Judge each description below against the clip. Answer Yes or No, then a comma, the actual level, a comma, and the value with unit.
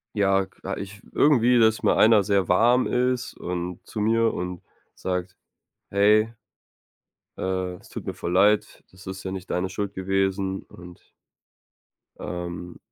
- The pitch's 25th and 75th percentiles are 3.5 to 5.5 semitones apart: No, average, 2.9 semitones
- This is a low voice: Yes, very low, 95 Hz